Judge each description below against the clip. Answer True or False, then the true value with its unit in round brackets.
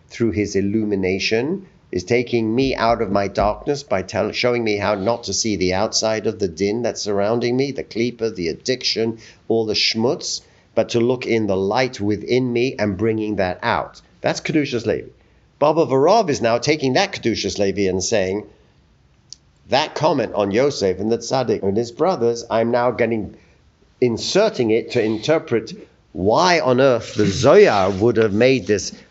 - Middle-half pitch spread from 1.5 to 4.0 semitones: True (2.9 semitones)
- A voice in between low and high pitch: False (115 Hz)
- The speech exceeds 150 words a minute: True (175 wpm)